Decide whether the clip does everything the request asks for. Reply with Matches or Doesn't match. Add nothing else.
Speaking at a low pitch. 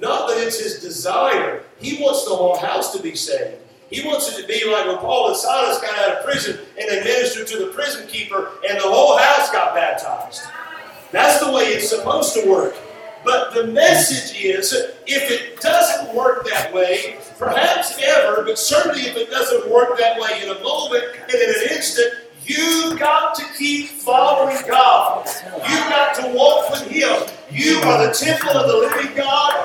Doesn't match